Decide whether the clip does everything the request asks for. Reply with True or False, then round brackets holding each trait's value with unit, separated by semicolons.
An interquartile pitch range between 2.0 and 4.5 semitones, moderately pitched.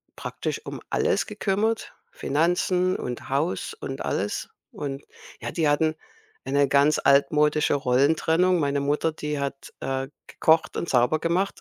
True (2.9 semitones; 150 Hz)